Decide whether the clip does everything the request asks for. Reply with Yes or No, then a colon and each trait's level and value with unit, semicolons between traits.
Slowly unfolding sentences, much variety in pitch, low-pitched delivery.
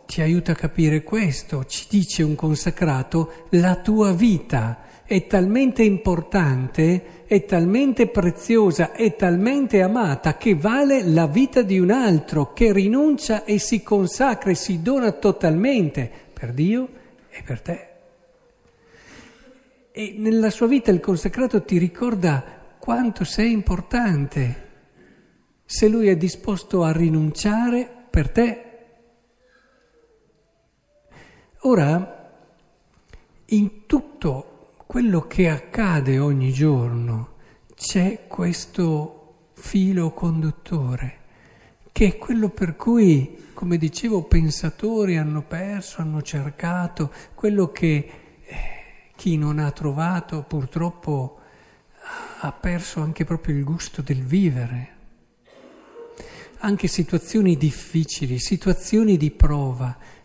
No: slow, 105 wpm; wide, 5.8 semitones; medium, 180 Hz